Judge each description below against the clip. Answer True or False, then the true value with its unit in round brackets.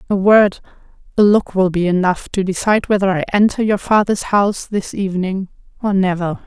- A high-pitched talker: True (195 Hz)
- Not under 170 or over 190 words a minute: True (175 wpm)